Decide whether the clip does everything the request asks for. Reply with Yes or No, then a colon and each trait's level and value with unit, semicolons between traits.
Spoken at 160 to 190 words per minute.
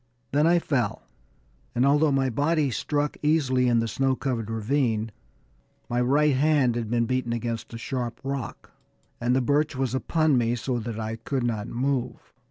Yes: average, 175 wpm